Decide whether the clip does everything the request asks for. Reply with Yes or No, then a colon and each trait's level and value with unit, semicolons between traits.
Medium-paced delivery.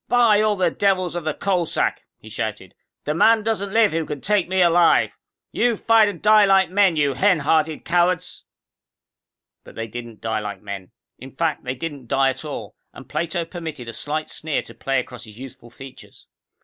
Yes: average, 195 wpm